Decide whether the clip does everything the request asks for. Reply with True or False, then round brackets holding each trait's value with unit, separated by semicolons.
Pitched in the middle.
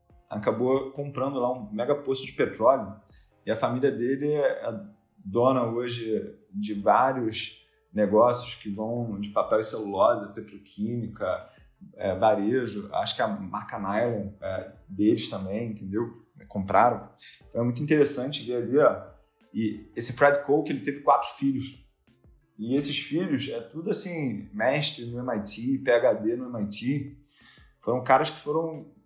False (130 Hz)